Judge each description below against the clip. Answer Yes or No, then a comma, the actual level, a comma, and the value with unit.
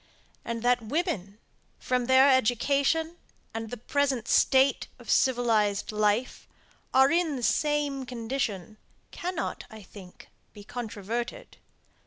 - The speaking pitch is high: Yes, high, 245 Hz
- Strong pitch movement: No, average, 4.0 semitones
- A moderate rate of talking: No, slow, 115 wpm